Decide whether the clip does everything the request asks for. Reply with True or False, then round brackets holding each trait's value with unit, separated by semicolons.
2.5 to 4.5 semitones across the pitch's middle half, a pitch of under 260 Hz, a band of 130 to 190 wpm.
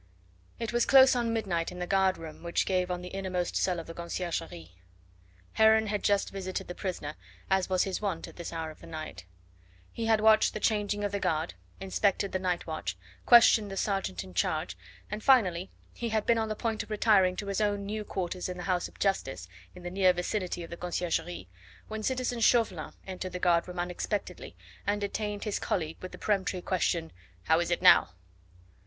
False (3.3 semitones; 185 Hz; 205 wpm)